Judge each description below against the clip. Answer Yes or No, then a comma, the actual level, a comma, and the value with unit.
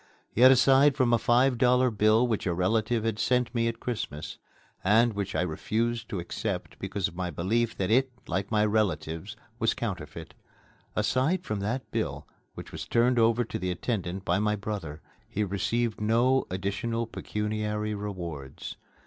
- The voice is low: Yes, low, 110 Hz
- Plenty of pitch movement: No, average, 3.7 semitones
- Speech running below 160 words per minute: No, average, 165 wpm